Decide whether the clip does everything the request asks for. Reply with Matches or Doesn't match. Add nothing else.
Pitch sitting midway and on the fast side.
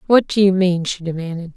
Matches